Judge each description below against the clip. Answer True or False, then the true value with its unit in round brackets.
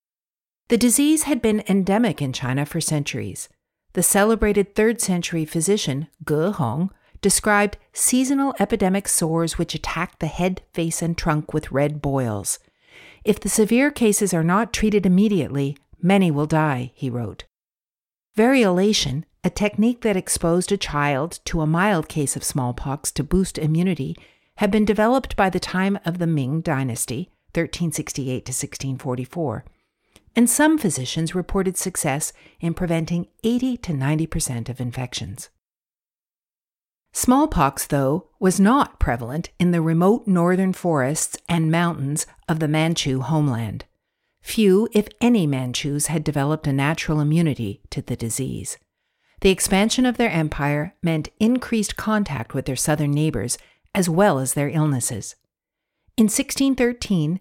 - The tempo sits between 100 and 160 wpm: True (140 wpm)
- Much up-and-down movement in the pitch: True (6.0 semitones)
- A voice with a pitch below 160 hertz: False (165 Hz)